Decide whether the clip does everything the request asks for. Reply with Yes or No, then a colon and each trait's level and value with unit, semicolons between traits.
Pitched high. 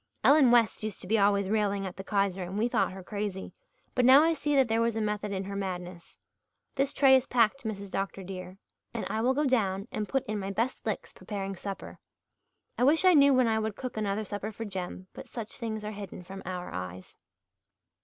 Yes: high, 210 Hz